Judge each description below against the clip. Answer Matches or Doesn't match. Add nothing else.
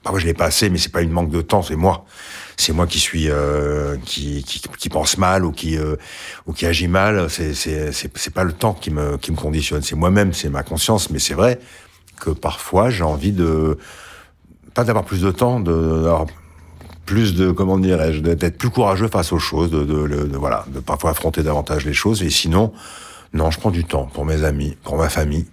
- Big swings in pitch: Doesn't match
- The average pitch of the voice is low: Matches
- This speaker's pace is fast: Matches